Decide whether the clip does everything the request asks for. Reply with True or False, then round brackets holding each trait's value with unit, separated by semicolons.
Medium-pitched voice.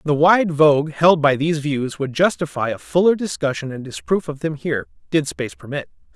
True (150 Hz)